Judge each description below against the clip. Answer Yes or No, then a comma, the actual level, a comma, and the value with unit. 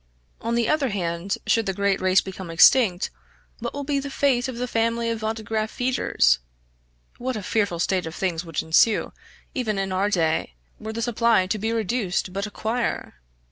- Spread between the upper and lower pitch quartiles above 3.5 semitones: Yes, average, 4.0 semitones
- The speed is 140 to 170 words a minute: No, average, 185 wpm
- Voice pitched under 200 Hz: No, high, 215 Hz